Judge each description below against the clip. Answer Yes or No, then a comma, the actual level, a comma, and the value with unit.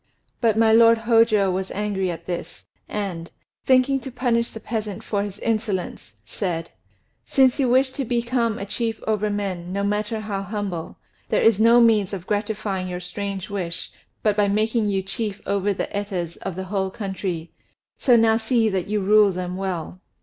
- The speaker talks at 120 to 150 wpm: No, average, 180 wpm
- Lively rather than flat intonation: No, average, 2.9 semitones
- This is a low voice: No, high, 205 Hz